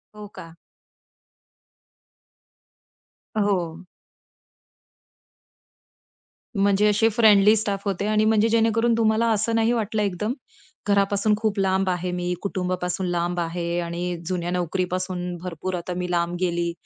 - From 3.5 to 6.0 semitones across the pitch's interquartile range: No, average, 3.1 semitones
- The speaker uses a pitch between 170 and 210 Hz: Yes, high, 190 Hz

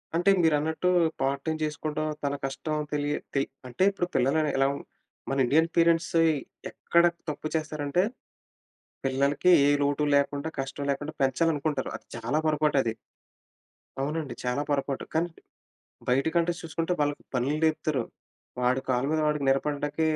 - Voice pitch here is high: No, medium, 150 Hz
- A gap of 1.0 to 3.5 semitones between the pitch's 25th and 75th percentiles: Yes, narrow, 2.5 semitones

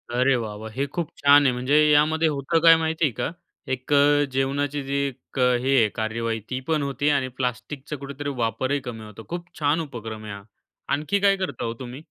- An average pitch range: Yes, average, 3.3 semitones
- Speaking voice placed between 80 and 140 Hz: Yes, low, 135 Hz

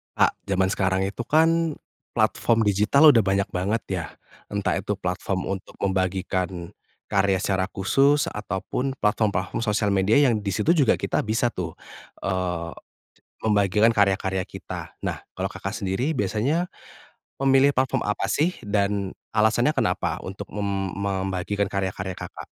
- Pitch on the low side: Yes, low, 100 Hz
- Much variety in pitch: No, average, 3.1 semitones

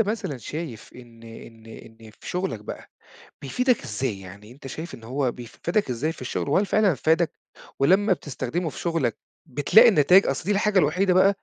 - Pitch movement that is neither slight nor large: No, wide, 7.8 semitones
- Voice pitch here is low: No, medium, 150 Hz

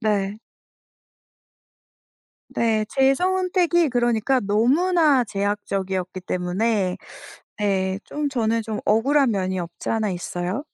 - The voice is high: Yes, high, 220 Hz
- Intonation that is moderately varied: No, wide, 5.7 semitones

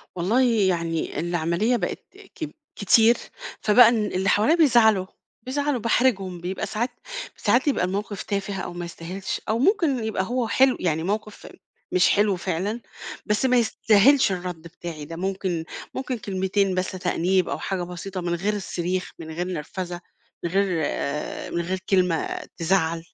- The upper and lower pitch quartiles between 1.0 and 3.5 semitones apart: No, average, 4.1 semitones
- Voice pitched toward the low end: No, high, 190 Hz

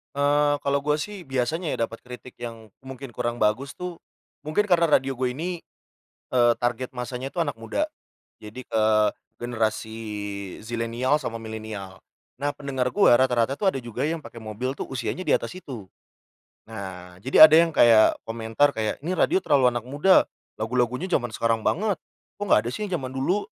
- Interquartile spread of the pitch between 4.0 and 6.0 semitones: Yes, average, 4.4 semitones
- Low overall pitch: Yes, low, 125 Hz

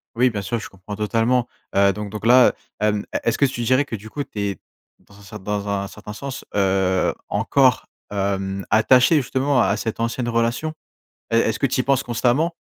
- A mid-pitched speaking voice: No, low, 115 Hz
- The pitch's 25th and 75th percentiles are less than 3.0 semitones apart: No, average, 3.9 semitones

